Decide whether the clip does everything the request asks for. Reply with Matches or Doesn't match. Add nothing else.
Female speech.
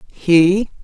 Matches